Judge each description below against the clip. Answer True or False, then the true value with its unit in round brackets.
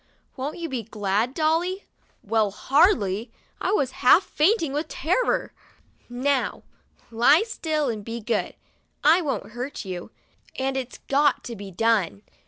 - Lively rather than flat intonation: True (5.7 semitones)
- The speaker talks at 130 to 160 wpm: True (140 wpm)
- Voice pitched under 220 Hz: False (265 Hz)